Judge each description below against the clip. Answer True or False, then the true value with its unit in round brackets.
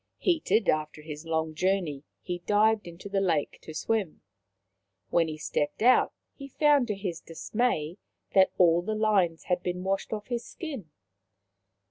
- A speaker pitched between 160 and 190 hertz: True (185 Hz)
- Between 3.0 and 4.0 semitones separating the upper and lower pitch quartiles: False (4.9 semitones)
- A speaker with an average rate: True (155 wpm)